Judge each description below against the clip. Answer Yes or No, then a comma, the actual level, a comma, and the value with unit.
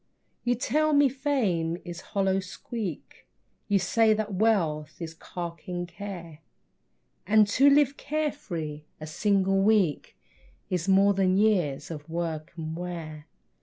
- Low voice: No, high, 190 Hz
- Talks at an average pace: No, slow, 130 wpm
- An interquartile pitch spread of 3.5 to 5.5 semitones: Yes, average, 4.8 semitones